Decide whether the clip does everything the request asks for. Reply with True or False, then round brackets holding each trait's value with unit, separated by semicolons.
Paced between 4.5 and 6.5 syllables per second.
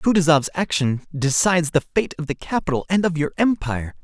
True (5.7 syllables/s)